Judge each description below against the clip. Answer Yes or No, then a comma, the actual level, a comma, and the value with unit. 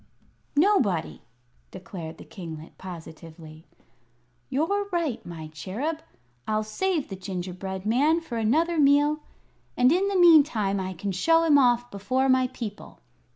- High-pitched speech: Yes, high, 230 Hz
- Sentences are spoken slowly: Yes, slow, 130 wpm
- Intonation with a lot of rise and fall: Yes, wide, 8.6 semitones